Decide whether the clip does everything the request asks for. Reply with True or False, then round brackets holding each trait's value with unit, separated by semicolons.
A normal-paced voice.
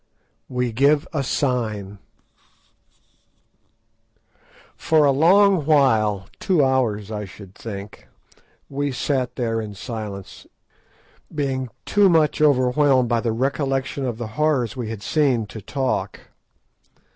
False (110 wpm)